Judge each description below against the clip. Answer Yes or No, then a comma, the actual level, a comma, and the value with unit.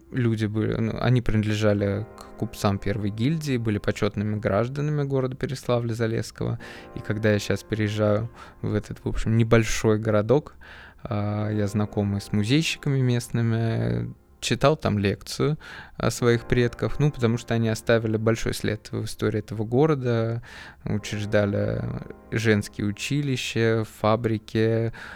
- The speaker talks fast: No, average, 125 wpm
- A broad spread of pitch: No, narrow, 2.4 semitones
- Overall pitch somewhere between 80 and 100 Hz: No, low, 110 Hz